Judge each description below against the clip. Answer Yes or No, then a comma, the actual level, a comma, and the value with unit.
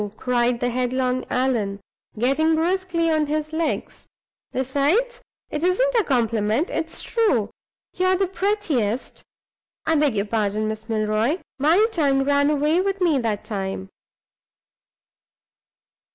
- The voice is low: No, very high, 280 Hz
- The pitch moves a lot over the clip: Yes, wide, 6.4 semitones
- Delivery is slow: Yes, slow, 125 wpm